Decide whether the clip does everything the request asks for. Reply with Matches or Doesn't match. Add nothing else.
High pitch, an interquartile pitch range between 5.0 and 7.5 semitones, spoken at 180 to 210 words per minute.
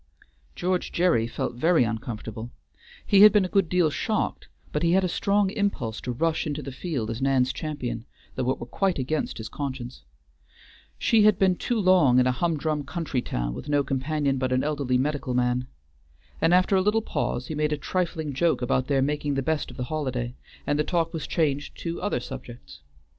Doesn't match